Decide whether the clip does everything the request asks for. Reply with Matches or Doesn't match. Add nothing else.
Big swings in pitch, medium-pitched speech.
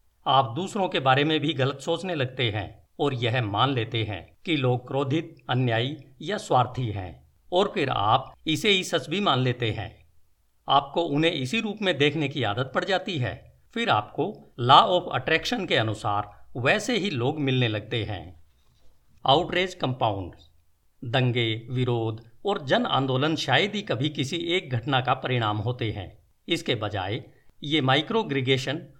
Doesn't match